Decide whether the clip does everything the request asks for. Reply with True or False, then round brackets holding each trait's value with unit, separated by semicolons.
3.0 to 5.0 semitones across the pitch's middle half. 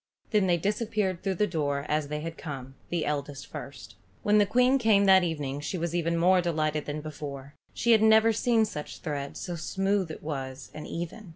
False (5.4 semitones)